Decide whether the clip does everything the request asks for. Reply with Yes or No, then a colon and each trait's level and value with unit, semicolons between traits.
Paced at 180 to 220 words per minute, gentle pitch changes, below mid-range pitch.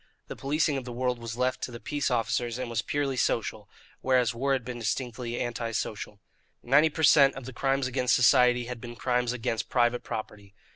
Yes: average, 200 wpm; narrow, 2.0 semitones; low, 125 Hz